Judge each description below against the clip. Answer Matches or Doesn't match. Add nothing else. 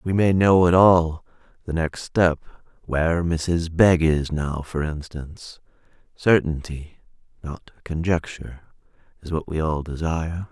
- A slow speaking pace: Matches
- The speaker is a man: Matches